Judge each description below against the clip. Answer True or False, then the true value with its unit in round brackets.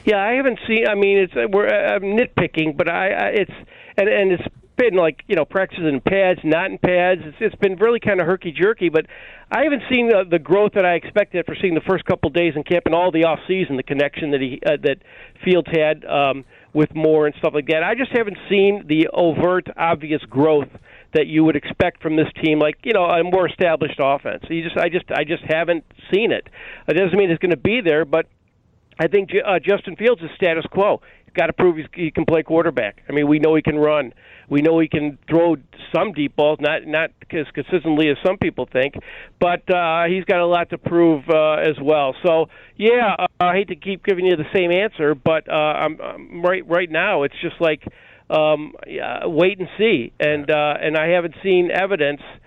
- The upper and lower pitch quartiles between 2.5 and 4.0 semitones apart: True (3.3 semitones)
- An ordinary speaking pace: False (225 wpm)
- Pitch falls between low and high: True (170 Hz)